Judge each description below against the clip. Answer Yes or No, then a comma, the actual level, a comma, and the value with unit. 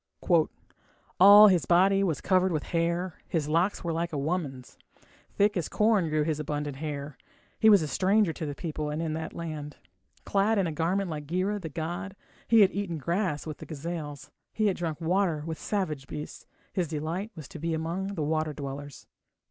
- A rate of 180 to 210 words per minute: Yes, average, 190 wpm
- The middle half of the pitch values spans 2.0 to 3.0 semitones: No, average, 3.7 semitones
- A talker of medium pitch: Yes, medium, 165 Hz